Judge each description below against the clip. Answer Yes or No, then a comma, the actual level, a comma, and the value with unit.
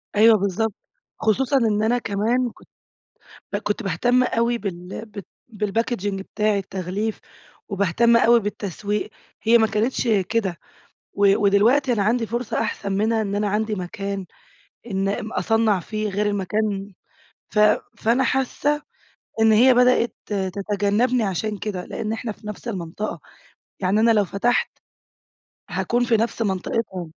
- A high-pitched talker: Yes, high, 215 Hz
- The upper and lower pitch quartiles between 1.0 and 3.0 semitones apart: Yes, narrow, 2.6 semitones